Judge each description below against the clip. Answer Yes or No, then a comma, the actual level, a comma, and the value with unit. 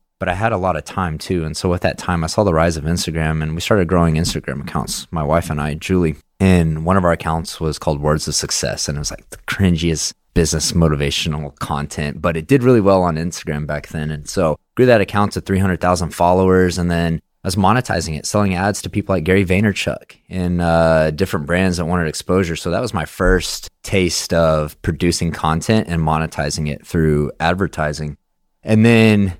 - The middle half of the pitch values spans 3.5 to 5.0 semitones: No, average, 3.1 semitones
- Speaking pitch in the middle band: No, very low, 85 Hz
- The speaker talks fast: Yes, fast, 210 wpm